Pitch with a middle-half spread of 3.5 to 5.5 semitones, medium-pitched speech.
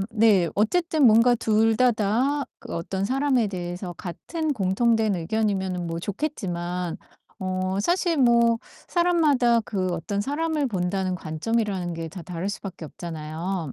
No: average, 5.2 semitones; high, 205 Hz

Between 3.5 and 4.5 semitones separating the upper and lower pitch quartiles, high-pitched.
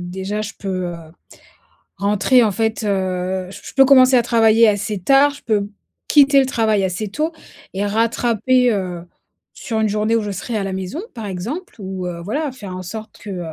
Yes: average, 4.1 semitones; high, 215 Hz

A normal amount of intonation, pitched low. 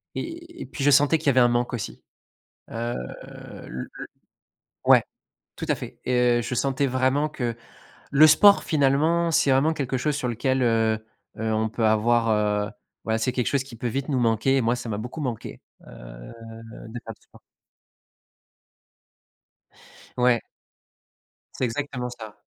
Yes: average, 3.5 semitones; low, 125 Hz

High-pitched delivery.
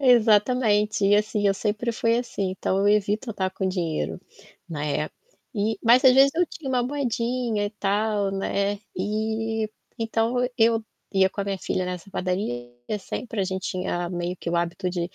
Yes: high, 205 Hz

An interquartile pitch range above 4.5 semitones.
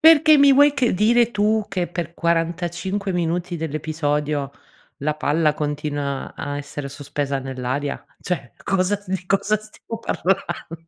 Yes: wide, 5.4 semitones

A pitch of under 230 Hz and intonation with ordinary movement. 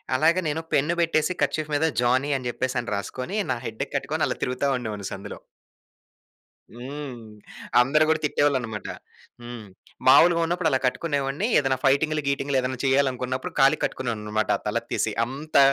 Yes: low, 135 Hz; average, 3.7 semitones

